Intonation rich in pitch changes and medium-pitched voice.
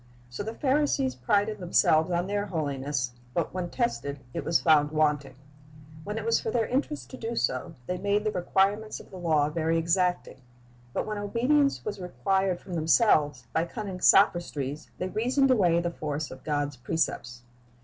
Yes: wide, 5.9 semitones; medium, 175 Hz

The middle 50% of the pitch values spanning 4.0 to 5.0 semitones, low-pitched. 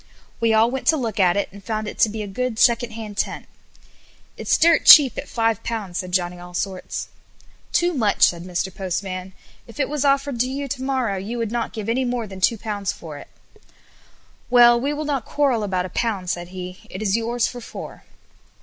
No: average, 4.6 semitones; high, 220 Hz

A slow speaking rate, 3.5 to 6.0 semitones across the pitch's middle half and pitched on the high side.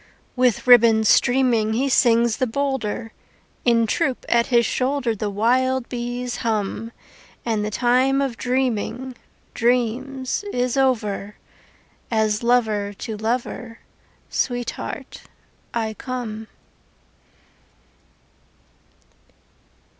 No: slow, 95 wpm; narrow, 2.5 semitones; high, 240 Hz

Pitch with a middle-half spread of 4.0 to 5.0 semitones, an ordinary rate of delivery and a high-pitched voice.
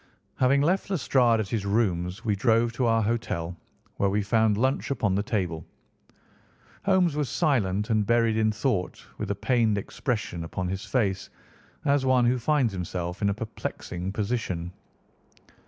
No: average, 4.3 semitones; average, 155 wpm; low, 110 Hz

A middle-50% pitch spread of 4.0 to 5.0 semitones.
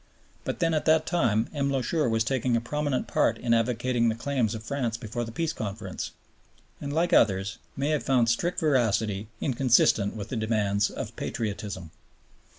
Yes: average, 4.3 semitones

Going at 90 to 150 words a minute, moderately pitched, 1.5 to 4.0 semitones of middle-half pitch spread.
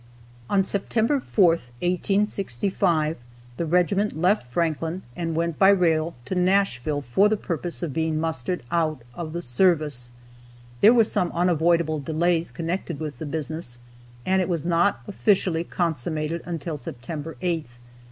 Yes: average, 140 wpm; medium, 170 Hz; average, 2.7 semitones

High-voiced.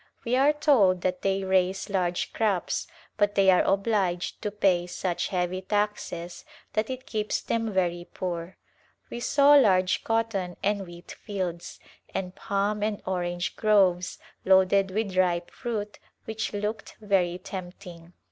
Yes: high, 195 Hz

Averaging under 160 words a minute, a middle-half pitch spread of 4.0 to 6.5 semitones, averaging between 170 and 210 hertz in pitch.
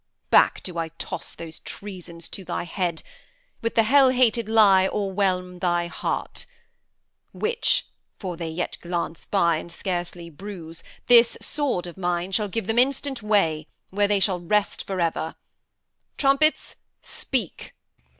Yes: average, 140 wpm; average, 4.5 semitones; high, 190 Hz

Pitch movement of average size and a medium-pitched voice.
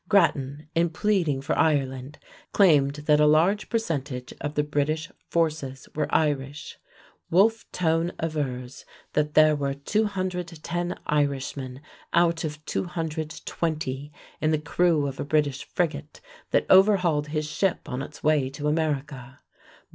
Yes: average, 3.0 semitones; medium, 150 Hz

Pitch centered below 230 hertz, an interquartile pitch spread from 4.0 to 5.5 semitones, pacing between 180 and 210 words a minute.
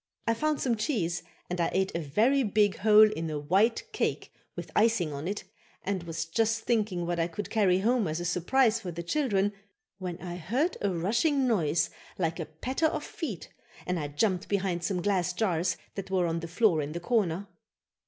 Yes: high, 190 Hz; average, 4.7 semitones; average, 200 wpm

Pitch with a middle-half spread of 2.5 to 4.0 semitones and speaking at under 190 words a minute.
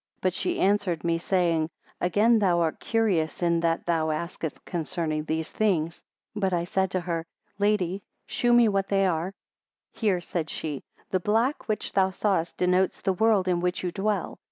Yes: average, 3.1 semitones; average, 180 wpm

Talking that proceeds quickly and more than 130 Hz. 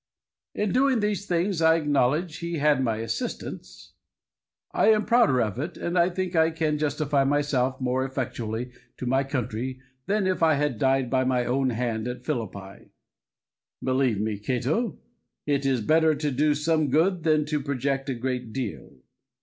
No: average, 165 wpm; medium, 140 Hz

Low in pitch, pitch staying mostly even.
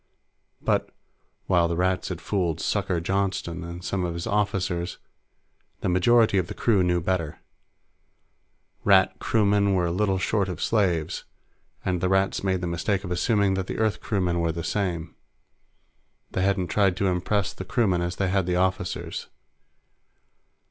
Yes: very low, 95 Hz; narrow, 2.1 semitones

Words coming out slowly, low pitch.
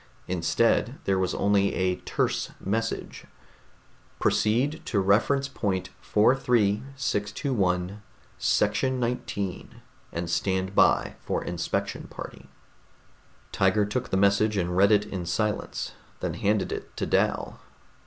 Yes: slow, 115 wpm; low, 100 Hz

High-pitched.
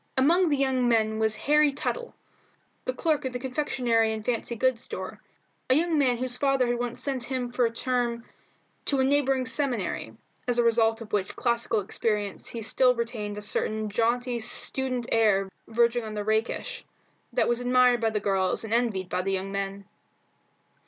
Yes: high, 240 Hz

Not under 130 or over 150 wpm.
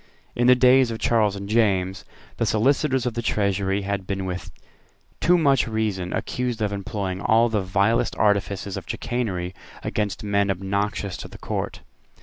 No: average, 160 wpm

